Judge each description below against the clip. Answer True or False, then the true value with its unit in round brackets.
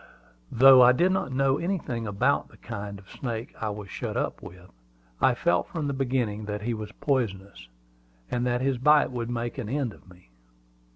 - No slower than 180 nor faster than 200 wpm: True (190 wpm)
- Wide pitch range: False (4.4 semitones)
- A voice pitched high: False (120 Hz)